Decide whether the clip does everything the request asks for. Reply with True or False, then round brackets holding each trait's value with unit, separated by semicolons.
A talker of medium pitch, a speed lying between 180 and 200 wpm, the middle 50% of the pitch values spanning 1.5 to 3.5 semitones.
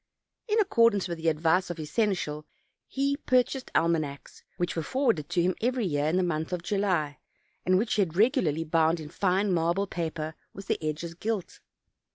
False (175 Hz; 190 wpm; 4.5 semitones)